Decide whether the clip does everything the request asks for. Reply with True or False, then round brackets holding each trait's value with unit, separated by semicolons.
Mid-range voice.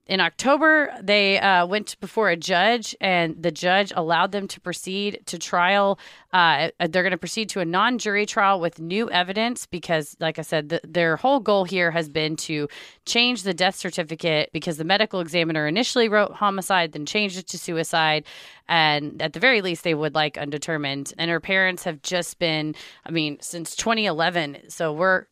True (175 Hz)